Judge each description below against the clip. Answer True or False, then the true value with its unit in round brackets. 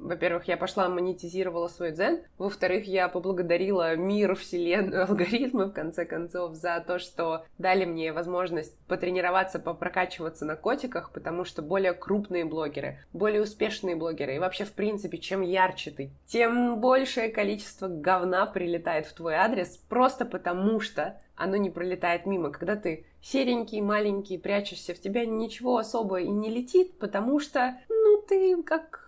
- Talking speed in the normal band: True (150 wpm)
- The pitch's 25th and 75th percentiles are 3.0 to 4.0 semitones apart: True (3.5 semitones)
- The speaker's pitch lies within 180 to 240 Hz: True (185 Hz)